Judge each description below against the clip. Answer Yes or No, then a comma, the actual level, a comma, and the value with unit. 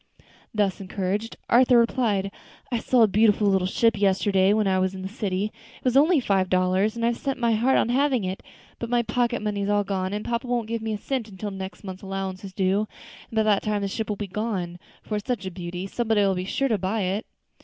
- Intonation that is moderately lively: Yes, average, 3.3 semitones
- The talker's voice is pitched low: No, high, 205 Hz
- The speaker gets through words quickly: Yes, fast, 235 wpm